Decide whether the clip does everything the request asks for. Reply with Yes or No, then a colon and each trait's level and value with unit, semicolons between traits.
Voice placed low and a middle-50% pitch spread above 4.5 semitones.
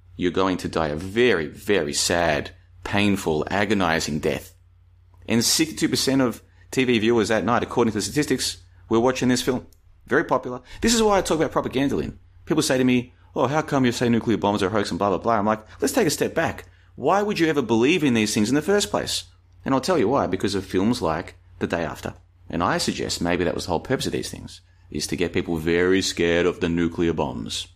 Yes: very low, 95 Hz; wide, 5.6 semitones